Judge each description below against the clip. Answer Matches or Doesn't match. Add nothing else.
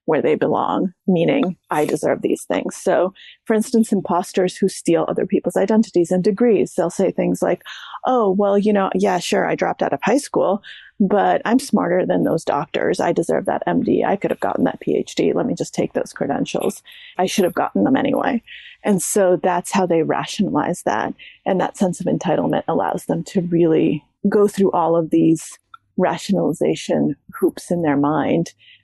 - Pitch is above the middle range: Matches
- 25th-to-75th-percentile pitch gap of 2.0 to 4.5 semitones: Matches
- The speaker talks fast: Doesn't match